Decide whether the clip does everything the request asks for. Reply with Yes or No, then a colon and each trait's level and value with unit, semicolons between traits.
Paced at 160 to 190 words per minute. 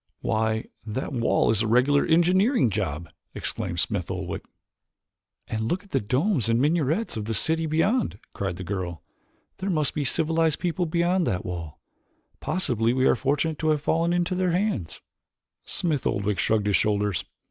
Yes: average, 170 wpm